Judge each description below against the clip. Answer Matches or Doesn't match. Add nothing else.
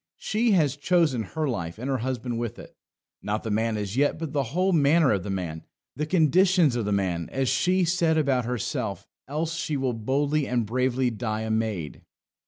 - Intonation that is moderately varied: Doesn't match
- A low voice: Matches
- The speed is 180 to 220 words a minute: Matches